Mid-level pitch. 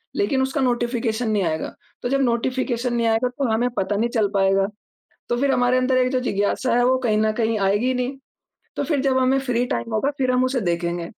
No: high, 245 Hz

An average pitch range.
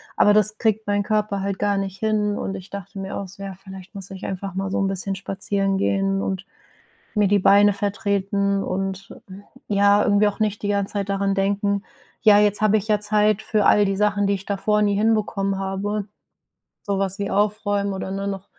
No: narrow, 1.0 semitones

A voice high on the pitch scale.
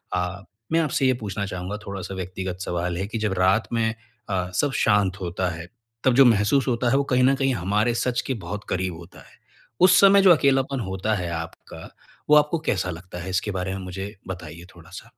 No: low, 100 Hz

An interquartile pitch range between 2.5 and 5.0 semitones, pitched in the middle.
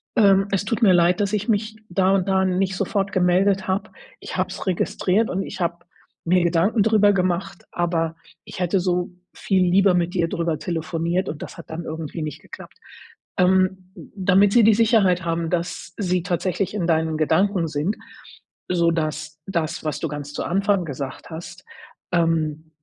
Yes: average, 2.8 semitones; medium, 180 Hz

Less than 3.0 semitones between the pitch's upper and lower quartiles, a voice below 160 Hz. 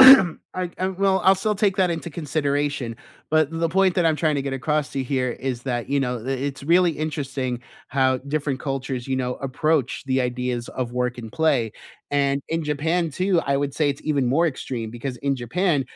No: average, 3.9 semitones; medium, 140 Hz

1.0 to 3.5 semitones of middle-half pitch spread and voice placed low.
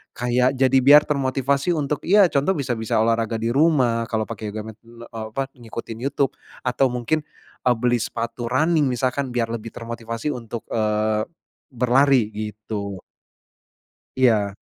Yes: average, 3.2 semitones; low, 120 Hz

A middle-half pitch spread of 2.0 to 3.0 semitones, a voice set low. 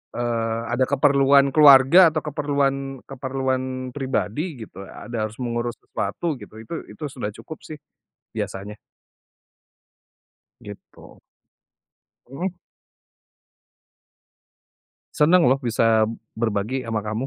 No: average, 3.6 semitones; low, 130 Hz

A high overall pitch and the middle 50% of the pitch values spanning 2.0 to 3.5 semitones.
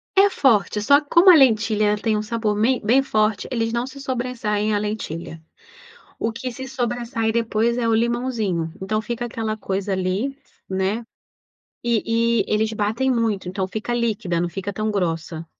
Yes: high, 220 Hz; average, 2.7 semitones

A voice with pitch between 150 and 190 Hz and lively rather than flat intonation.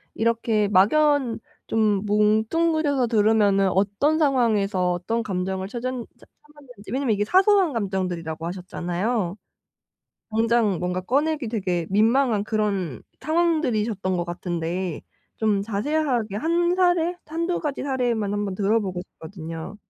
No: high, 215 Hz; wide, 6.0 semitones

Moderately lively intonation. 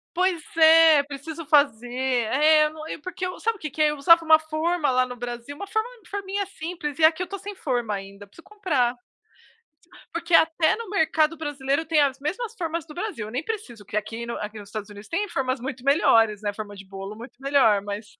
No: wide, 5.9 semitones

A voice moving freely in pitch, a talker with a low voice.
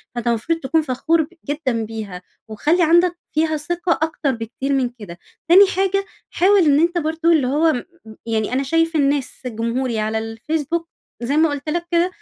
No: wide, 5.7 semitones; very high, 295 Hz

